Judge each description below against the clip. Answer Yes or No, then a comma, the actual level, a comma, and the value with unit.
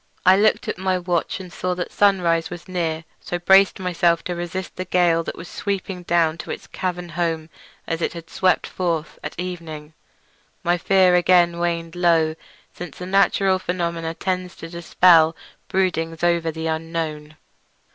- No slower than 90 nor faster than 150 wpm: No, average, 165 wpm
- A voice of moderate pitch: Yes, medium, 175 Hz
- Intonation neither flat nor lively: No, narrow, 1.8 semitones